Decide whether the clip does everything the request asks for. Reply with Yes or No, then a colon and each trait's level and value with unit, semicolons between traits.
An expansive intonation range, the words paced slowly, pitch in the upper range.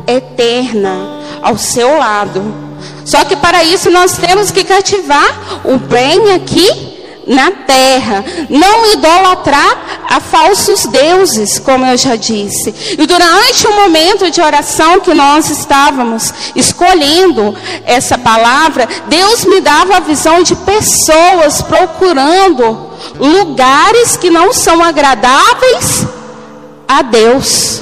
Yes: wide, 6.4 semitones; slow, 115 wpm; very high, 320 Hz